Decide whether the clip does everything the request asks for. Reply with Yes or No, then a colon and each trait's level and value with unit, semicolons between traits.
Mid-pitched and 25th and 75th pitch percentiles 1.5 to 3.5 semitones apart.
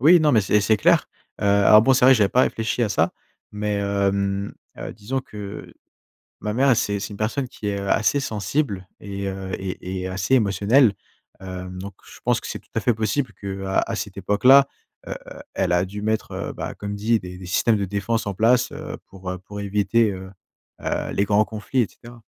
No: low, 105 Hz; average, 2.9 semitones